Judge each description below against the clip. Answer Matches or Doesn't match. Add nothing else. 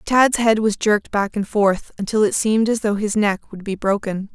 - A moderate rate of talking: Doesn't match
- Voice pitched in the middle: Doesn't match